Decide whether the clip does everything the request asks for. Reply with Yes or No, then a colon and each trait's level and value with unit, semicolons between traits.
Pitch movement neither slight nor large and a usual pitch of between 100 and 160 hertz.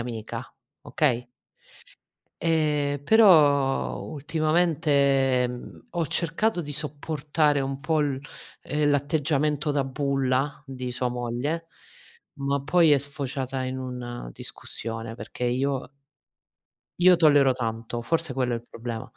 Yes: average, 3.2 semitones; medium, 140 Hz